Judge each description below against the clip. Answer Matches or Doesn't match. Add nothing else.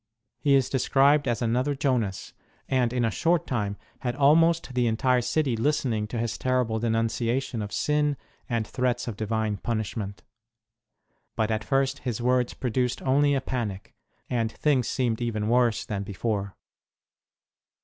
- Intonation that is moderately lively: Matches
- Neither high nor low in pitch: Doesn't match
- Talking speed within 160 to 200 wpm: Doesn't match